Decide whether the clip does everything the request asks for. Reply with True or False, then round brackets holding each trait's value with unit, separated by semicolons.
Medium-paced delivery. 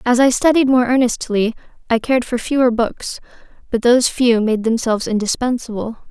True (155 wpm)